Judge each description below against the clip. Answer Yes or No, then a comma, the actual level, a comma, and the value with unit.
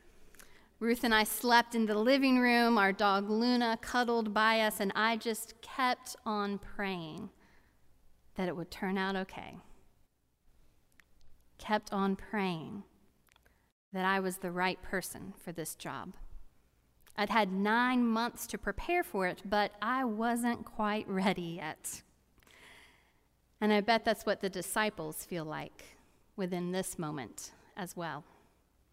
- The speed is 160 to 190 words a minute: No, slow, 135 wpm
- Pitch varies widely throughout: No, average, 3.6 semitones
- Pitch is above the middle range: Yes, high, 205 Hz